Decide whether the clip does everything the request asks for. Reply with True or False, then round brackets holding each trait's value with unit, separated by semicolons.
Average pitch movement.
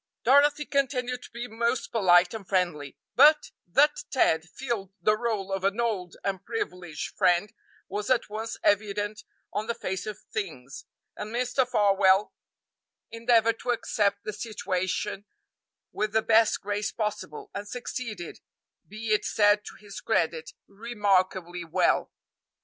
True (3.5 semitones)